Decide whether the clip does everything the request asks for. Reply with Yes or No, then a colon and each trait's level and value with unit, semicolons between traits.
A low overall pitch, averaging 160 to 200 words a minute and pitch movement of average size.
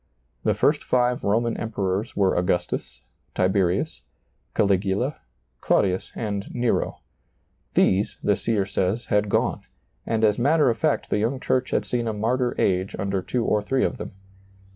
No: low, 105 Hz; average, 150 wpm; average, 3.7 semitones